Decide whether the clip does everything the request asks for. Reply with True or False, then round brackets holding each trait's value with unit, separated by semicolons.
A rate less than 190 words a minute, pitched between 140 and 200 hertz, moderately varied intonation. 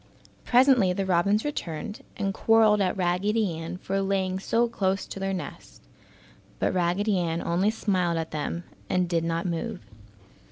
True (155 wpm; 190 Hz; 3.2 semitones)